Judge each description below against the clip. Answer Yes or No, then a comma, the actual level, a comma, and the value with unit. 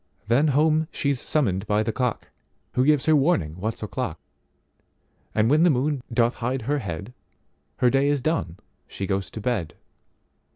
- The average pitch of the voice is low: Yes, low, 125 Hz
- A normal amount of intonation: No, wide, 6.0 semitones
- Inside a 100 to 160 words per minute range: Yes, average, 150 wpm